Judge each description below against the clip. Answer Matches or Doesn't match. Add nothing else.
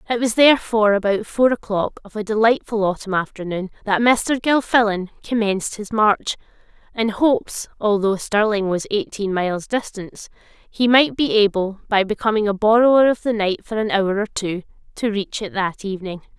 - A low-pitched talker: Doesn't match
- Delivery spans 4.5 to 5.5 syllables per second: Matches